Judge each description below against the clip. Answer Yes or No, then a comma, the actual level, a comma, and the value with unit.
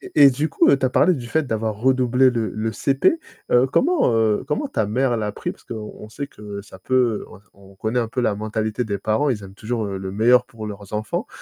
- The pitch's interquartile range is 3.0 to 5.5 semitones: Yes, average, 3.4 semitones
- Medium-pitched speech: No, low, 115 Hz